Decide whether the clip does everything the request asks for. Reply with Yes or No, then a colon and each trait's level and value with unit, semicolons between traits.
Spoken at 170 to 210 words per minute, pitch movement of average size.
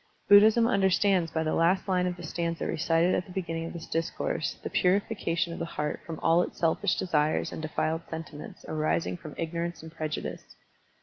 No: average, 185 wpm; narrow, 2.1 semitones